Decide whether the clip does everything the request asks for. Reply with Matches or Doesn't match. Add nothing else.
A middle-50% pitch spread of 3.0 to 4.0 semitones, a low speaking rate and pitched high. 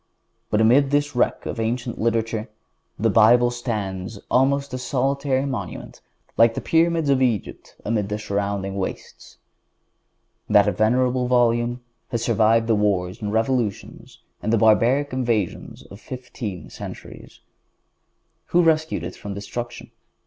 Doesn't match